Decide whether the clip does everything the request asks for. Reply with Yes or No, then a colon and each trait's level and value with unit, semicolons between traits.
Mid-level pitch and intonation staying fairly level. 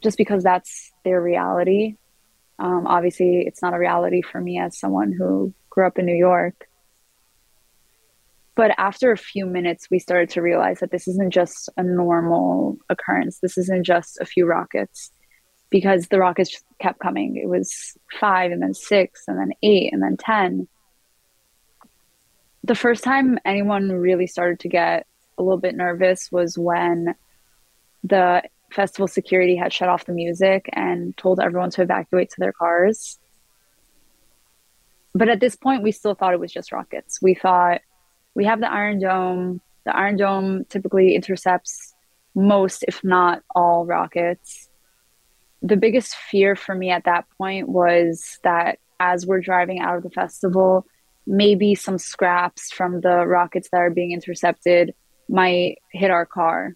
Yes: medium, 180 Hz; narrow, 1.7 semitones